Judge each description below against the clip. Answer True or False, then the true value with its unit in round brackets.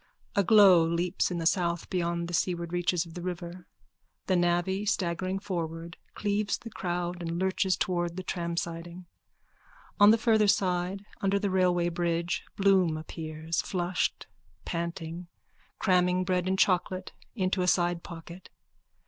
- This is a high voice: False (175 Hz)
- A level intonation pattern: True (1.7 semitones)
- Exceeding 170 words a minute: False (140 wpm)